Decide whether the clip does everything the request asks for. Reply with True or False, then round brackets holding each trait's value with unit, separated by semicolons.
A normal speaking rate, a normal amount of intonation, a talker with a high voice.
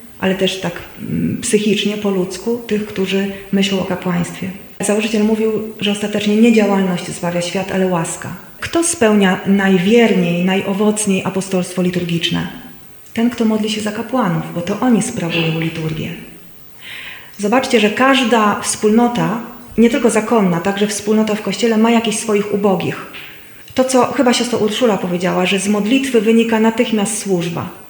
True (140 wpm; 3.1 semitones; 205 Hz)